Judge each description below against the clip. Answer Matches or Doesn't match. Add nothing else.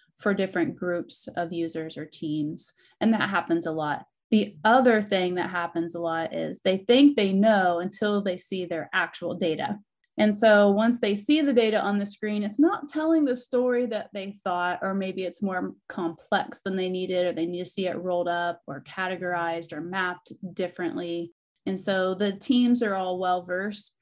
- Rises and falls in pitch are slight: Doesn't match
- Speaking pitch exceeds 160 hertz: Matches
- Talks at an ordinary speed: Matches